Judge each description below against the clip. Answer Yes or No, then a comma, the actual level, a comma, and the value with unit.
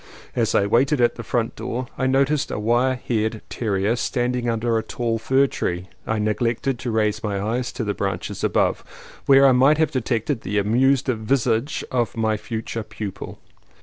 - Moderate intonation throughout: Yes, average, 3.0 semitones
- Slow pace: No, average, 180 wpm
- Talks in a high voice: No, low, 115 Hz